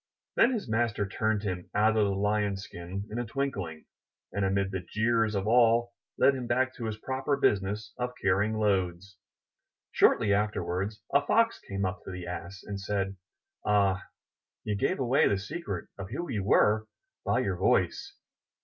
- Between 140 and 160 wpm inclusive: No, average, 170 wpm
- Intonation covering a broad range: No, average, 3.4 semitones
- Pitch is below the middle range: Yes, low, 105 Hz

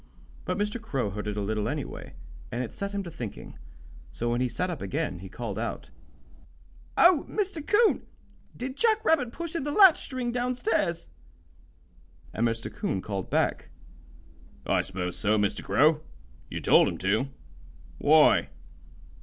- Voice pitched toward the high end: No, medium, 160 Hz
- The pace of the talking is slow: No, average, 160 wpm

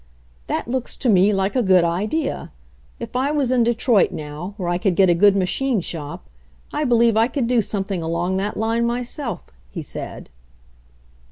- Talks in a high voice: Yes, high, 210 Hz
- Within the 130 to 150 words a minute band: No, average, 180 wpm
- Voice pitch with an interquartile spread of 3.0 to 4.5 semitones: No, average, 4.9 semitones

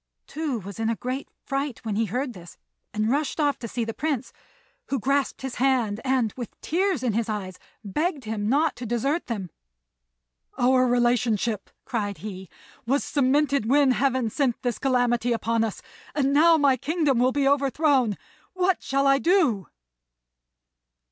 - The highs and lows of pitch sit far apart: No, average, 3.9 semitones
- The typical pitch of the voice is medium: No, very high, 255 Hz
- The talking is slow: No, average, 160 wpm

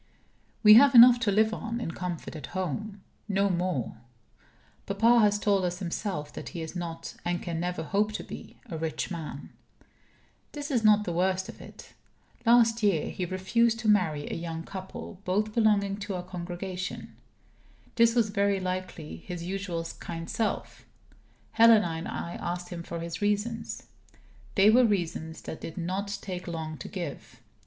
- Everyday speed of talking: Yes, average, 165 wpm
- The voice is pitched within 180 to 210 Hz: Yes, high, 190 Hz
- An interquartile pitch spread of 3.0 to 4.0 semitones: Yes, average, 3.7 semitones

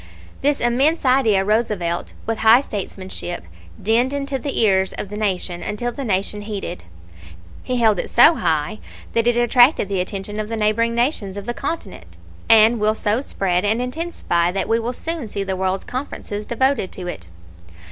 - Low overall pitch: No, high, 215 Hz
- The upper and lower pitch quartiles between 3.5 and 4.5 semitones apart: Yes, average, 3.9 semitones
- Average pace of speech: Yes, average, 175 wpm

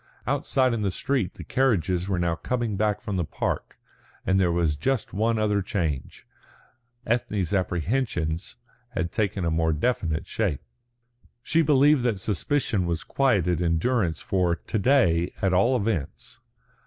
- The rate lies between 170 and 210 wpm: No, average, 150 wpm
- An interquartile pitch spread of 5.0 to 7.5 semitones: Yes, wide, 5.6 semitones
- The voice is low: Yes, very low, 95 Hz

